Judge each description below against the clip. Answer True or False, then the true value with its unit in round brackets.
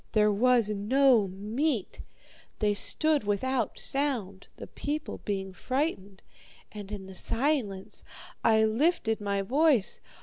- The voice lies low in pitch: False (220 Hz)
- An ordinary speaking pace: False (115 wpm)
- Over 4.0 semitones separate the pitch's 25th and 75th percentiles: True (5.3 semitones)